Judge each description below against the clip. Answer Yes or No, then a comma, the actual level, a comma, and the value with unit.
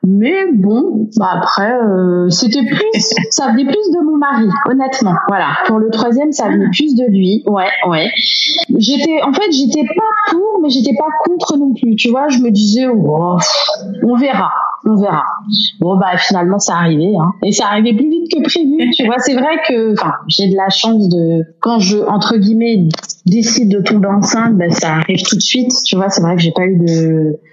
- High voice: Yes, high, 220 Hz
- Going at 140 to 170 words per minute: No, average, 205 wpm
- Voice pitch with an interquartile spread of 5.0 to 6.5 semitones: Yes, wide, 5.6 semitones